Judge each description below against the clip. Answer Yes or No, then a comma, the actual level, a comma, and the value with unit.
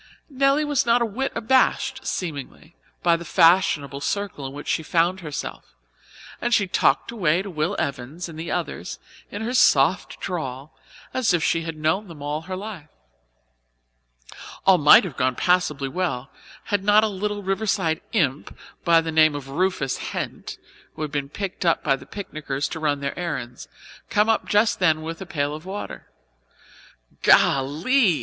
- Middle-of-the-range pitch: Yes, medium, 170 Hz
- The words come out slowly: No, average, 165 wpm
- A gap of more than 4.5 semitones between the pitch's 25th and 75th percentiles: Yes, wide, 5.5 semitones